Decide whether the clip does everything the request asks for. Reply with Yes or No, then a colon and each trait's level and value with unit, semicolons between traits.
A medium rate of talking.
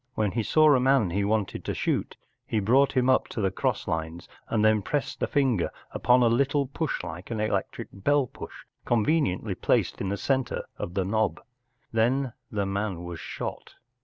Yes: average, 190 wpm